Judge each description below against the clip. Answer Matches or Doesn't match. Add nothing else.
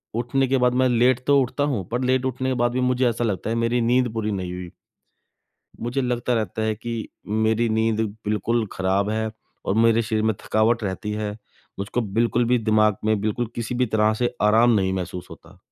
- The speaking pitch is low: Matches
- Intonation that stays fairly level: Matches